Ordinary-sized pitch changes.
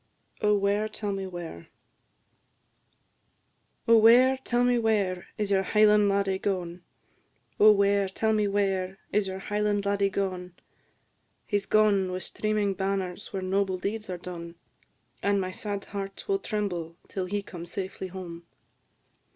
No: narrow, 2.0 semitones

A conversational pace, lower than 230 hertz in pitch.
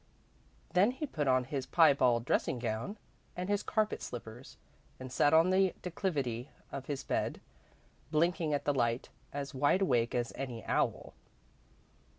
Yes: average, 150 wpm; medium, 140 Hz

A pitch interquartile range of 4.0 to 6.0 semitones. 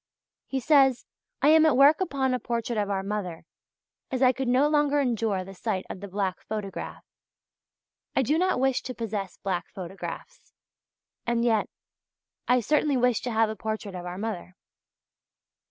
Yes: average, 5.0 semitones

